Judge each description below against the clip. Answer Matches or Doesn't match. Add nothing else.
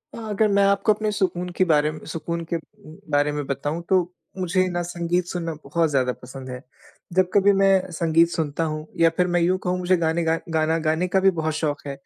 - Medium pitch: Matches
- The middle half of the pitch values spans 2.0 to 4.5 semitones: Matches